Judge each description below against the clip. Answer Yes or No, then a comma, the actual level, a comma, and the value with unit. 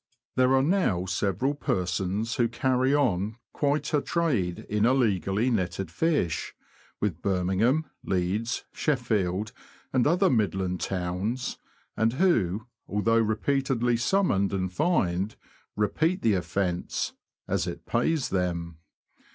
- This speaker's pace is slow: Yes, slow, 115 wpm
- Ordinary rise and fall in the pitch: No, wide, 6.1 semitones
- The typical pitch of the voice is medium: No, low, 110 Hz